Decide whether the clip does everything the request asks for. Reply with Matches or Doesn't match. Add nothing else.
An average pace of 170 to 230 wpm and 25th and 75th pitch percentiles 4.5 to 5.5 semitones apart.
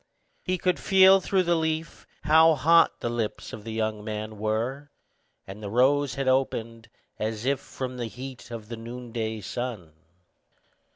Doesn't match